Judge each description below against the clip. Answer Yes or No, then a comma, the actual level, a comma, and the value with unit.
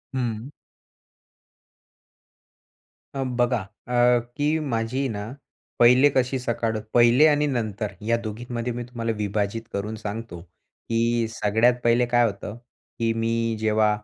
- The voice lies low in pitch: Yes, low, 115 Hz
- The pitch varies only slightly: Yes, narrow, 1.8 semitones